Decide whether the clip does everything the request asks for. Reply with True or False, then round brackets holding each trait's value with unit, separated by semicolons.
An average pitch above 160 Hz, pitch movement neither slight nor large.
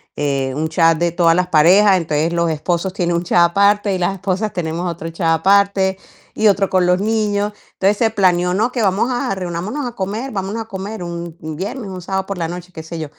True (185 Hz; 3.1 semitones)